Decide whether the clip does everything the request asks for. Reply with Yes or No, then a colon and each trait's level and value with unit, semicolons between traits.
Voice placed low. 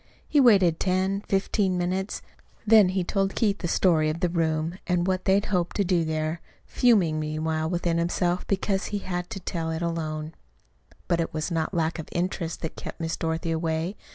No: medium, 175 Hz